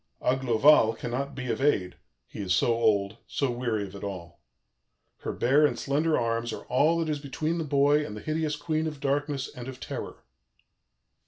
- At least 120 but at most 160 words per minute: No, average, 185 wpm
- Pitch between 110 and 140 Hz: Yes, low, 135 Hz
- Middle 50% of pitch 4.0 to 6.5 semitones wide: Yes, average, 4.5 semitones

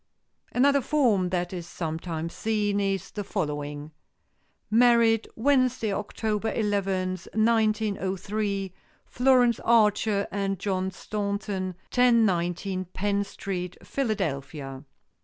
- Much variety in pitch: No, average, 3.2 semitones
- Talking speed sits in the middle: No, slow, 90 wpm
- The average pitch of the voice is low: No, high, 200 Hz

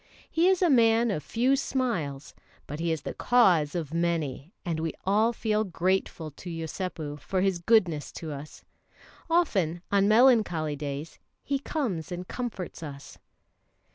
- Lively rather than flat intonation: Yes, wide, 6.3 semitones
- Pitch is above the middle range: No, medium, 180 Hz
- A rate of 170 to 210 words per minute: No, average, 150 wpm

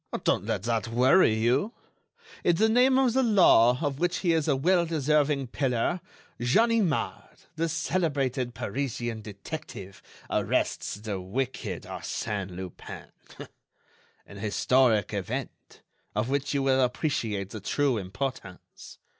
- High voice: No, low, 130 Hz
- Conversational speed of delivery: No, slow, 125 wpm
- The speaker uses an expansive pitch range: Yes, wide, 6.7 semitones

